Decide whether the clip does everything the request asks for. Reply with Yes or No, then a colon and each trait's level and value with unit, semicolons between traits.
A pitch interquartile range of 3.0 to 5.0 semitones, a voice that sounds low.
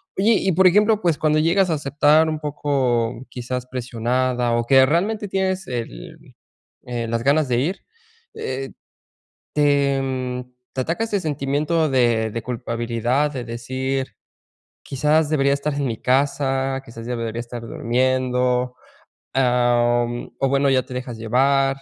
Yes: average, 3.5 semitones; low, 130 Hz